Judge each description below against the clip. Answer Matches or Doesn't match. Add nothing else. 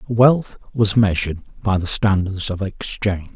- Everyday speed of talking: Matches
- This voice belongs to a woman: Doesn't match